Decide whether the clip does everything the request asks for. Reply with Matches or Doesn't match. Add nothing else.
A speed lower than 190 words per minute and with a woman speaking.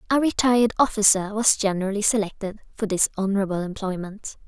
Matches